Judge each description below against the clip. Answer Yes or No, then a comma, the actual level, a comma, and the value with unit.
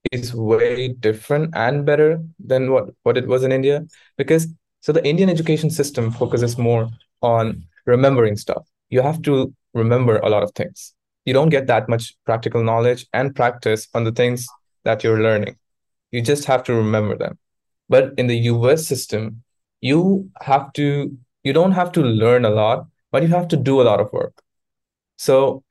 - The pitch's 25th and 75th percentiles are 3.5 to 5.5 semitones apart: Yes, average, 4.2 semitones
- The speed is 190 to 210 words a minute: No, average, 180 wpm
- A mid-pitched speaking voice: No, low, 125 Hz